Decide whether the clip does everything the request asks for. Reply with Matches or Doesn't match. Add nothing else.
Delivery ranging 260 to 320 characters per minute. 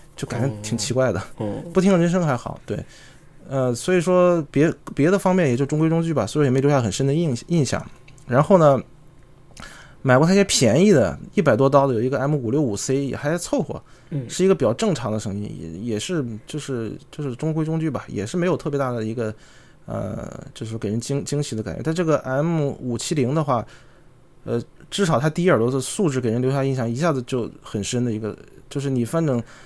Matches